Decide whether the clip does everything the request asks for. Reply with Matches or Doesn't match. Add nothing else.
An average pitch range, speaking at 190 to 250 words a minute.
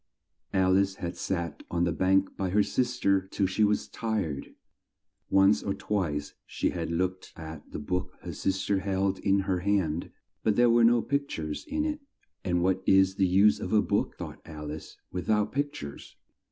Matches